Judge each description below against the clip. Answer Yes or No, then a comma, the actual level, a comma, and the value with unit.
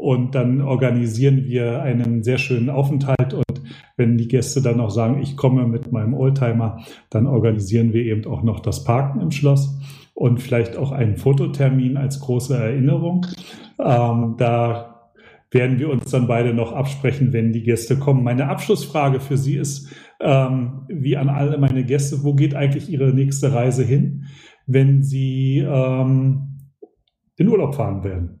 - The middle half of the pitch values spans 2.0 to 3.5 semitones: Yes, narrow, 2.6 semitones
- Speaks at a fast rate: No, average, 160 wpm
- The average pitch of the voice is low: Yes, low, 130 Hz